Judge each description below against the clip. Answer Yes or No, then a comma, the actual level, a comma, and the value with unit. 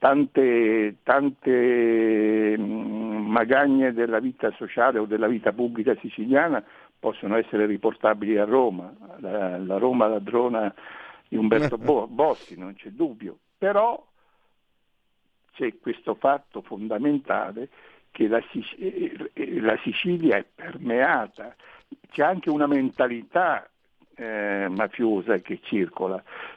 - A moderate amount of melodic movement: No, wide, 5.7 semitones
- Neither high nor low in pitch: No, low, 120 Hz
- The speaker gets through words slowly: Yes, slow, 105 wpm